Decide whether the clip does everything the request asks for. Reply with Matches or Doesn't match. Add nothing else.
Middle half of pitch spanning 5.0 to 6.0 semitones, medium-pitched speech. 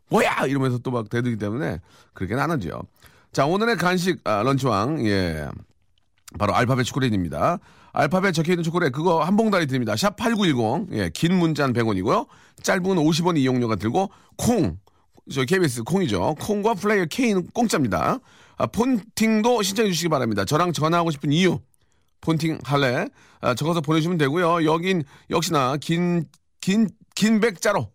Doesn't match